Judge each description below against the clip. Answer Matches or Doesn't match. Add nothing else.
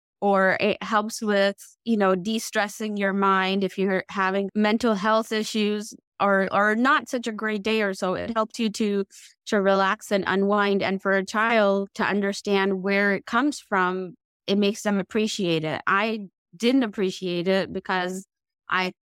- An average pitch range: Doesn't match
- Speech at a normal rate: Matches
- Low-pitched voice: Doesn't match